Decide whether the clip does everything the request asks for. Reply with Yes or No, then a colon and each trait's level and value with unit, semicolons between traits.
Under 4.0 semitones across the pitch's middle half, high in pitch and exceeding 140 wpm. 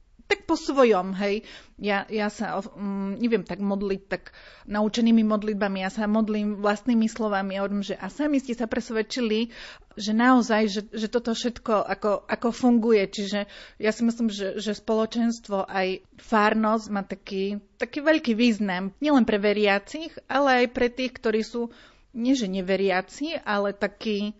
Yes: average, 2.8 semitones; high, 215 Hz; average, 155 wpm